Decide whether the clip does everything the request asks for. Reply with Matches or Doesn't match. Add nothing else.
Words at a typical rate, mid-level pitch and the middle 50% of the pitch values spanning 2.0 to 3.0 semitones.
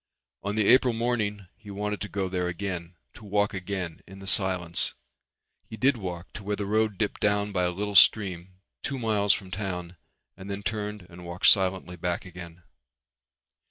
Doesn't match